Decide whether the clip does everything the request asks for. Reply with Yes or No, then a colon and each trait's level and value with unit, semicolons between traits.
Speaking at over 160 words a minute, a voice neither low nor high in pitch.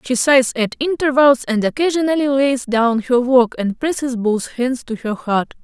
No: average, 180 wpm; very high, 255 Hz